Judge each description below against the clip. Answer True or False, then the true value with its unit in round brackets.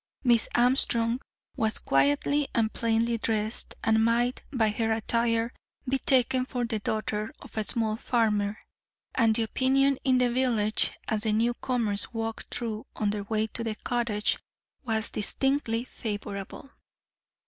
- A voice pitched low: False (225 Hz)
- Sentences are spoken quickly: False (140 wpm)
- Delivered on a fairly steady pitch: True (2.1 semitones)